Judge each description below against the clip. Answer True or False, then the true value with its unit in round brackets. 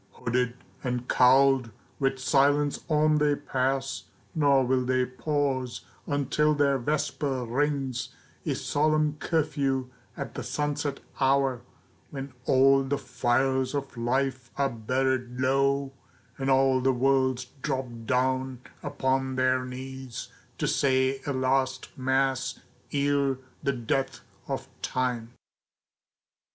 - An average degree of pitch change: False (1.4 semitones)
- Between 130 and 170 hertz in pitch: True (135 Hz)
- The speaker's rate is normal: False (115 wpm)